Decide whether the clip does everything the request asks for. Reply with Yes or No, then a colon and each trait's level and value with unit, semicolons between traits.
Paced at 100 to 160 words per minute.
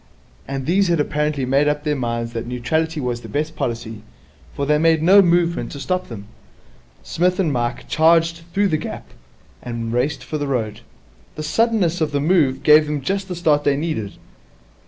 No: average, 185 wpm